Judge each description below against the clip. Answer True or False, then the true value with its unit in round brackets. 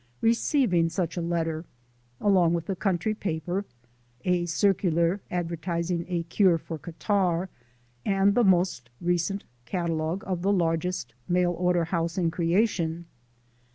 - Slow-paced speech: True (125 wpm)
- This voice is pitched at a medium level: True (175 Hz)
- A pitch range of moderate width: False (2.3 semitones)